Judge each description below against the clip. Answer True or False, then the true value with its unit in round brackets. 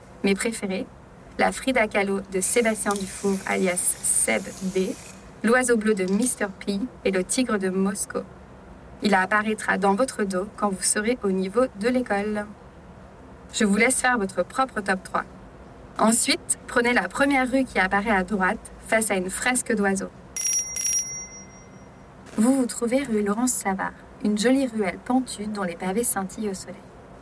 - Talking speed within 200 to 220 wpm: False (155 wpm)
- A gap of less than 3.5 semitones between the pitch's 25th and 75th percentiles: False (4.3 semitones)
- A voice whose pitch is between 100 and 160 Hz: False (210 Hz)